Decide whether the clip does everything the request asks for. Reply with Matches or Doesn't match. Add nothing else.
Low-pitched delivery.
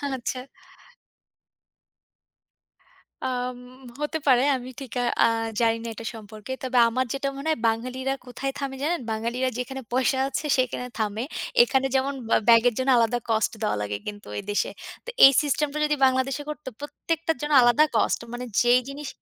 Doesn't match